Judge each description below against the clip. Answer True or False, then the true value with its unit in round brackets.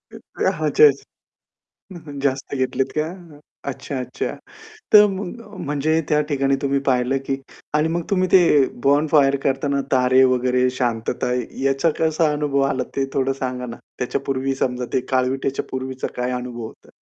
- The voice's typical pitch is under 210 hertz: True (135 Hz)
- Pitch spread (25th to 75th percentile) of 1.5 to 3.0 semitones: True (2.6 semitones)